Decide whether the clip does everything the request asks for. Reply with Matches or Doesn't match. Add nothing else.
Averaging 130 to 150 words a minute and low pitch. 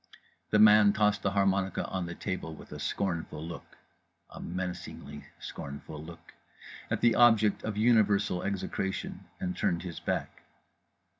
Matches